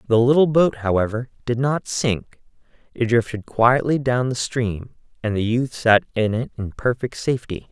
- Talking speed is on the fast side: No, average, 170 wpm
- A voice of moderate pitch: No, low, 120 Hz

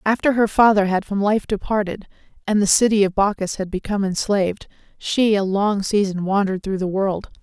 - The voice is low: No, high, 200 Hz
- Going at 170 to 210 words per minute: Yes, average, 185 wpm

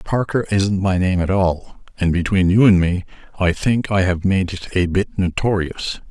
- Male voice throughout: Yes, male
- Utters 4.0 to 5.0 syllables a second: Yes, 4.5 syllables/s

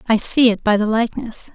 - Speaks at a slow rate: No, fast, 235 wpm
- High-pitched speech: Yes, high, 220 Hz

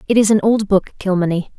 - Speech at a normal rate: No, fast, 225 wpm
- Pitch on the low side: No, high, 200 Hz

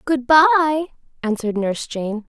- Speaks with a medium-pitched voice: No, very high, 260 Hz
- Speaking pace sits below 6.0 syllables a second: Yes, 5.8 syllables/s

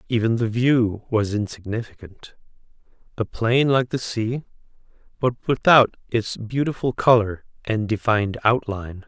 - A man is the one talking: Yes, male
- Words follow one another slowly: Yes, slow, 110 wpm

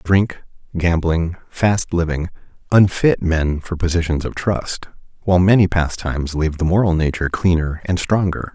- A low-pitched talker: Yes, very low, 85 Hz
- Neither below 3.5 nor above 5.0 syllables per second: Yes, 4.9 syllables/s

